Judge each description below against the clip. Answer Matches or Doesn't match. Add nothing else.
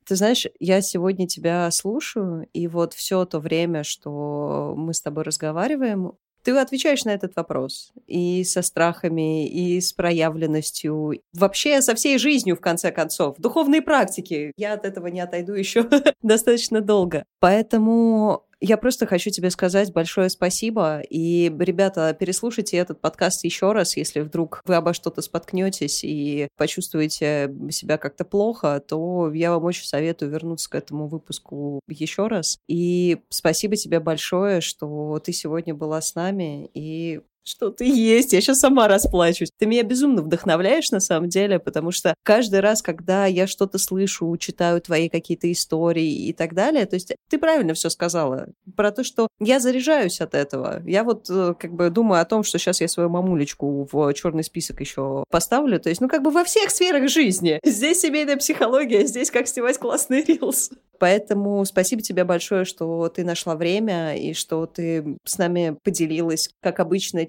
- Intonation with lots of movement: Doesn't match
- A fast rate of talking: Matches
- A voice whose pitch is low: Doesn't match